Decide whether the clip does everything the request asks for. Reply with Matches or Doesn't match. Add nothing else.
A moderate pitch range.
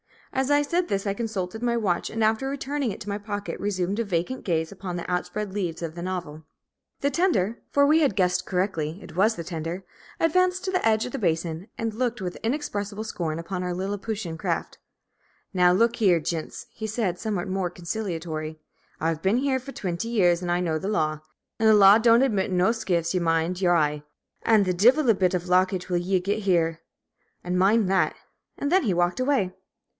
Matches